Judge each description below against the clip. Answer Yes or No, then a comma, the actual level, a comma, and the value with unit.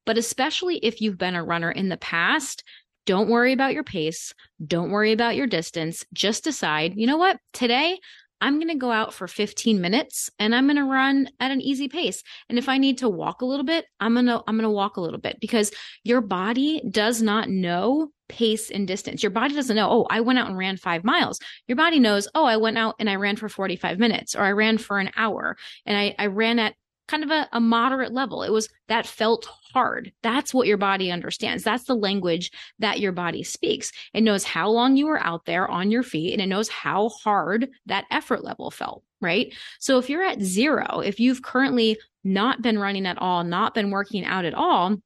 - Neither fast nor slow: No, fast, 220 wpm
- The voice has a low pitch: No, high, 220 Hz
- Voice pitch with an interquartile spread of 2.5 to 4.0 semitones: No, average, 4.5 semitones